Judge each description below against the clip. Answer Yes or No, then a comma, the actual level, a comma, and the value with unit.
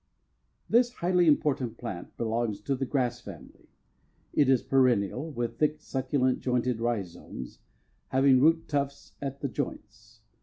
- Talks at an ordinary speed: No, slow, 130 wpm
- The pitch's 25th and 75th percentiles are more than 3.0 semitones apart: Yes, average, 3.5 semitones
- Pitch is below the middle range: Yes, low, 130 Hz